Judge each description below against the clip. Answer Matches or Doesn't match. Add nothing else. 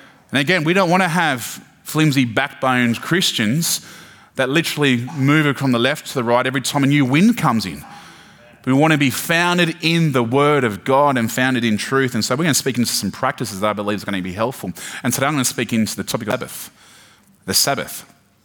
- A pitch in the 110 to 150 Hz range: Matches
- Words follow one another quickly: Matches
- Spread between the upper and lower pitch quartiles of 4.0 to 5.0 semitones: Matches